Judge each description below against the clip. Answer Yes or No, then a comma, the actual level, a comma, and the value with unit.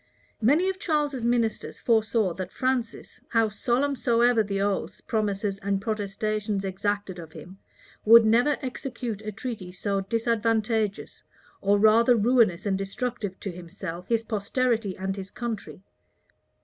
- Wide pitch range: No, average, 3.3 semitones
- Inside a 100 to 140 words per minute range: Yes, slow, 135 wpm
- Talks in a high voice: Yes, high, 215 Hz